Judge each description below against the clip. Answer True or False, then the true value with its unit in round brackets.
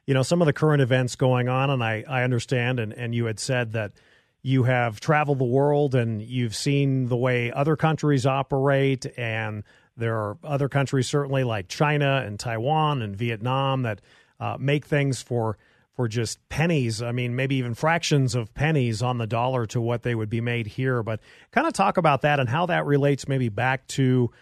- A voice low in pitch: True (130 Hz)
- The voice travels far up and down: False (2.9 semitones)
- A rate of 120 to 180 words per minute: False (200 wpm)